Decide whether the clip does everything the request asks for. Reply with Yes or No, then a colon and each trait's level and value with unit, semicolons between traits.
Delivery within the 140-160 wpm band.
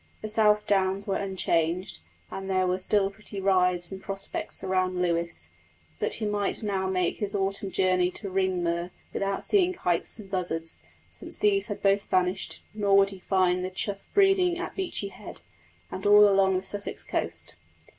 No: average, 170 wpm